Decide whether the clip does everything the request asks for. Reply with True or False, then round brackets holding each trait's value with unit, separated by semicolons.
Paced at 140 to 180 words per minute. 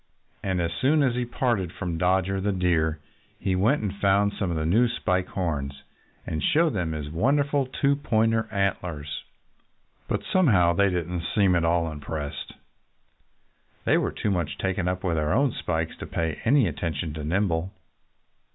True (170 wpm)